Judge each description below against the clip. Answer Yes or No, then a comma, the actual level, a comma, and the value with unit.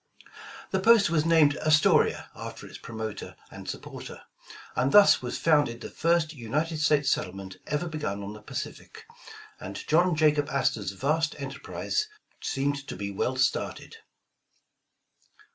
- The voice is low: No, medium, 145 Hz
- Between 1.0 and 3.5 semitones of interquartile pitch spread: No, wide, 5.4 semitones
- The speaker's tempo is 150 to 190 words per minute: No, slow, 135 wpm